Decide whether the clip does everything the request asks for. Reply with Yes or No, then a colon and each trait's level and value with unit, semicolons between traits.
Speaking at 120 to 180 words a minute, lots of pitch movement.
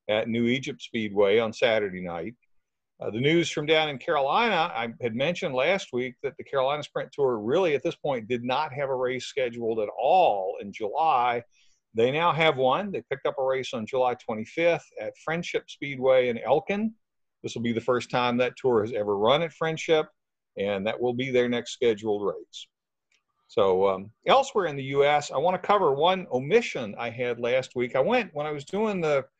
No: average, 200 wpm; wide, 6.8 semitones